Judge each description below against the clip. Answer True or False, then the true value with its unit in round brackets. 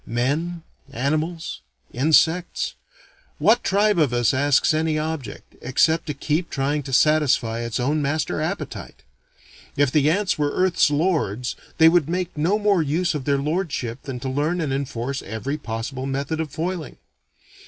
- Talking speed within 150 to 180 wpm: True (155 wpm)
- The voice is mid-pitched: True (150 Hz)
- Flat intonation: False (3.5 semitones)